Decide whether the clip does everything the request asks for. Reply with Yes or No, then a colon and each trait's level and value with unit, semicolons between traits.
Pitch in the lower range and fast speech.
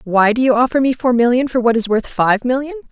No: high, 245 Hz; fast, 270 wpm